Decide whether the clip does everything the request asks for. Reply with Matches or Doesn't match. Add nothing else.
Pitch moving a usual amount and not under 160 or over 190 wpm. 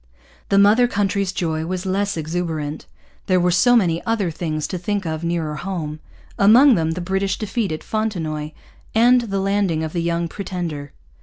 Matches